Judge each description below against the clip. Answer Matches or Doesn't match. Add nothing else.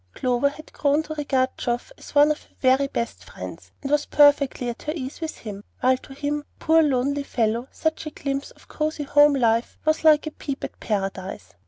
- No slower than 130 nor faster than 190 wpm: Doesn't match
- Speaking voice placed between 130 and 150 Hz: Doesn't match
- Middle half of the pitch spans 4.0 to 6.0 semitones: Doesn't match